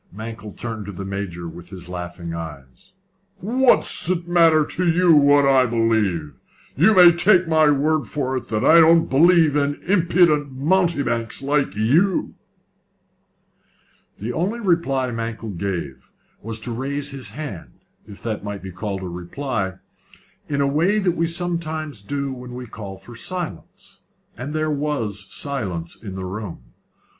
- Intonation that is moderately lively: No, wide, 8.0 semitones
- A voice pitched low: Yes, low, 130 Hz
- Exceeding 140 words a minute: Yes, average, 150 wpm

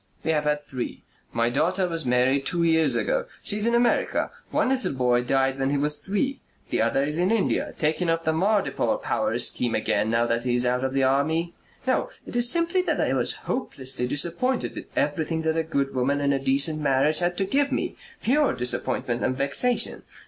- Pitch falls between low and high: Yes, medium, 150 Hz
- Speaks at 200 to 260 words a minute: Yes, fast, 205 wpm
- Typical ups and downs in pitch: No, wide, 5.7 semitones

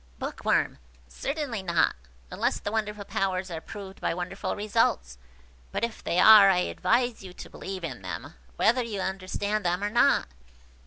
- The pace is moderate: Yes, average, 160 wpm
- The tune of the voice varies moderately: Yes, average, 3.1 semitones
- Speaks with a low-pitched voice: No, high, 195 Hz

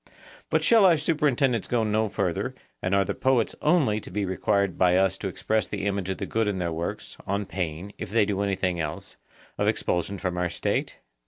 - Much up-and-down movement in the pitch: No, average, 3.2 semitones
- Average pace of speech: No, fast, 210 wpm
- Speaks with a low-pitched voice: Yes, low, 100 Hz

